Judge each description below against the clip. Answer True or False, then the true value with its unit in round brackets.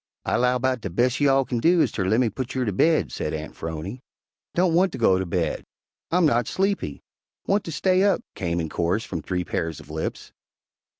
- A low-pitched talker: True (120 Hz)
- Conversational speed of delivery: False (220 wpm)